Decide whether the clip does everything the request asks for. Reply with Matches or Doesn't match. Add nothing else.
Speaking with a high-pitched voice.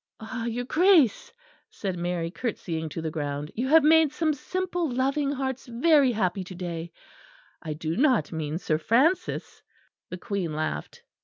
Matches